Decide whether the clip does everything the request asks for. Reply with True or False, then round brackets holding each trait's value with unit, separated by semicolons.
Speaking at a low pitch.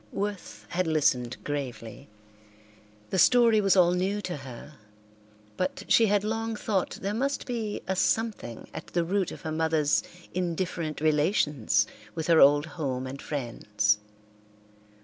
False (165 Hz)